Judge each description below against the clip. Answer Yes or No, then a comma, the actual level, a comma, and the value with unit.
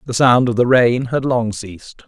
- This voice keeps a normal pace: No, fast, 230 wpm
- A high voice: No, low, 120 Hz